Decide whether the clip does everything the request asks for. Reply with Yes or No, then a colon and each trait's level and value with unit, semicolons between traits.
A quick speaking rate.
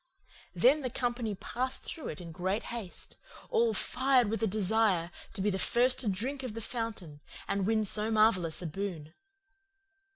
No: average, 165 wpm